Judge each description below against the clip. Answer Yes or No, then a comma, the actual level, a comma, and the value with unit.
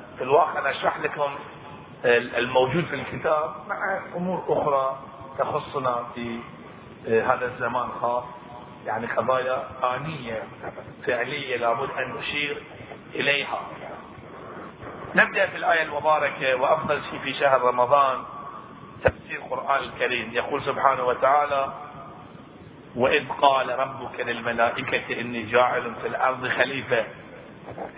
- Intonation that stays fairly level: No, average, 3.1 semitones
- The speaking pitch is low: Yes, low, 130 Hz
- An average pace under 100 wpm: No, average, 105 wpm